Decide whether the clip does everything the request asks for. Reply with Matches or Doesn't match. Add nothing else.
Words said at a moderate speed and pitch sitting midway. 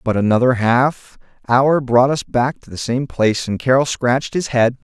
Doesn't match